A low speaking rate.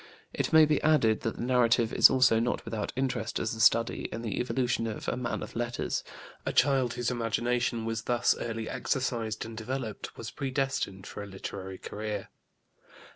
No: average, 180 wpm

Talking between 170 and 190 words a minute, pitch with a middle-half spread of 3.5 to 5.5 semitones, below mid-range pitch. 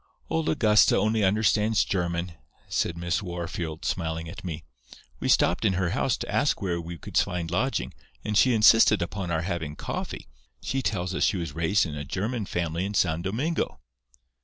Yes: average, 180 wpm; average, 3.9 semitones; very low, 90 Hz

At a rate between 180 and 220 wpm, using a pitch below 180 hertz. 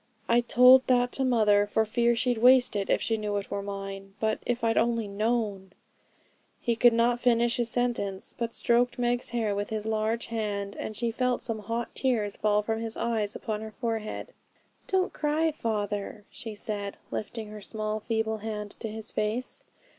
No: average, 185 wpm; high, 225 Hz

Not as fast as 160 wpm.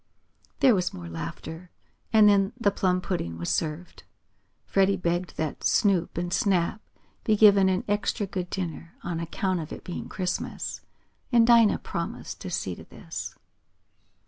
Yes: average, 150 wpm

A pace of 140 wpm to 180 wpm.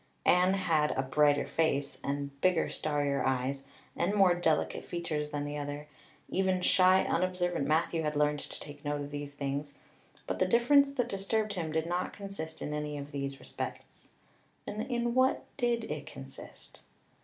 Yes: average, 165 wpm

